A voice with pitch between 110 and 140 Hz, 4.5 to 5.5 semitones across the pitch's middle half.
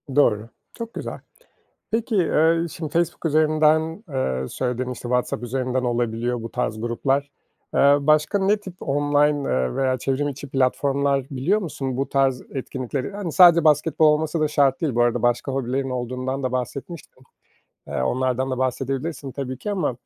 No: low, 135 Hz; average, 3.4 semitones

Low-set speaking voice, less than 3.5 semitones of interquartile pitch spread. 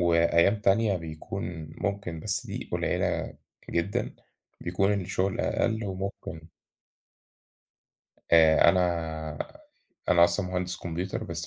Yes: very low, 90 Hz; average, 2.9 semitones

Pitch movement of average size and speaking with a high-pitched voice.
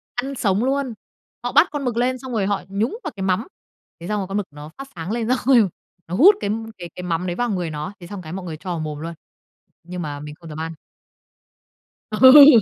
No: wide, 6.4 semitones; high, 195 Hz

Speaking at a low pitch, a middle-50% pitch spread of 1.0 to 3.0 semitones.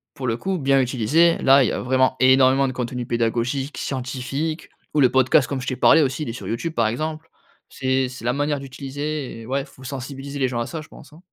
Yes: low, 130 Hz; narrow, 2.4 semitones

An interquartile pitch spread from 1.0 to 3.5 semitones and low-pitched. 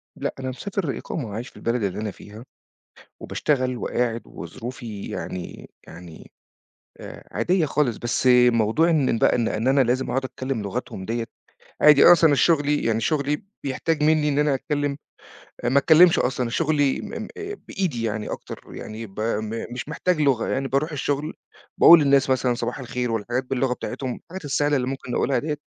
No: average, 4.2 semitones; low, 130 Hz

